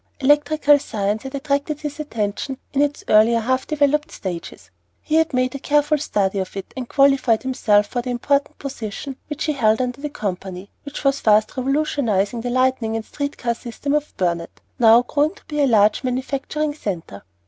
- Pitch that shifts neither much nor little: Yes, average, 5.0 semitones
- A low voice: No, very high, 260 Hz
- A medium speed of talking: Yes, average, 180 wpm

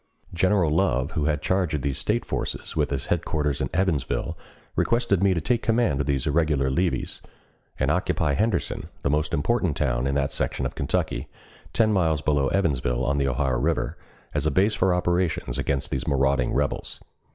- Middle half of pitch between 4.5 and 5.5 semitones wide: Yes, average, 5.1 semitones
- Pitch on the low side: Yes, very low, 75 Hz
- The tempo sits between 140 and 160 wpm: No, average, 180 wpm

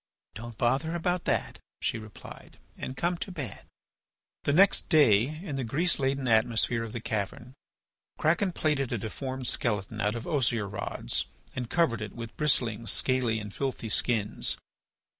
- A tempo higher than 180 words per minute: No, average, 155 wpm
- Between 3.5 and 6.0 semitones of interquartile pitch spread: Yes, average, 5.0 semitones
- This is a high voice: No, low, 120 Hz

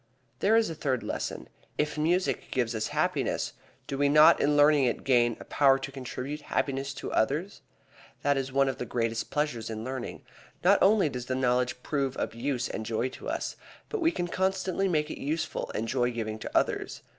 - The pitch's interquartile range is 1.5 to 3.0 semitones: No, average, 3.7 semitones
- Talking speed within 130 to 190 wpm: No, average, 200 wpm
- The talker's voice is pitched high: No, low, 135 Hz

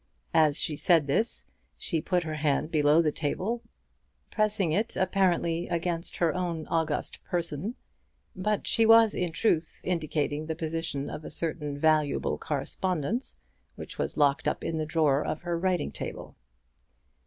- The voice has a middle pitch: Yes, medium, 165 Hz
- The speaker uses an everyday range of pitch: Yes, average, 3.1 semitones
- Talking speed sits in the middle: Yes, average, 150 wpm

